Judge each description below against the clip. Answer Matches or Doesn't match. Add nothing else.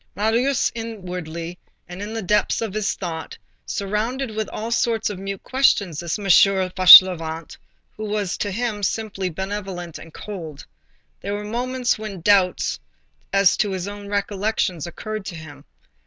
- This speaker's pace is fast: Doesn't match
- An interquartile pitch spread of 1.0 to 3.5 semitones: Matches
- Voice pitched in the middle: Doesn't match